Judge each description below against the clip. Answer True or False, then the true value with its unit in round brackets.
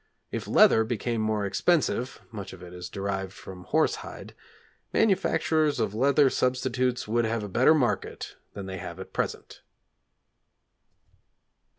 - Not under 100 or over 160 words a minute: True (135 wpm)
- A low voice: True (110 Hz)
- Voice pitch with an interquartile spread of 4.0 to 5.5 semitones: True (4.8 semitones)